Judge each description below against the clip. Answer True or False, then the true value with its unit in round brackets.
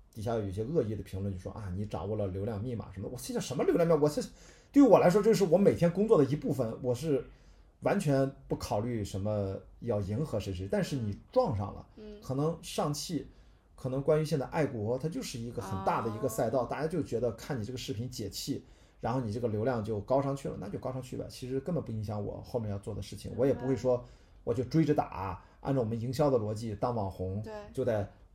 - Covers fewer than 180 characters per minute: False (350 characters per minute)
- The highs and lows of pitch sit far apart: False (4.8 semitones)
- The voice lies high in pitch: False (120 Hz)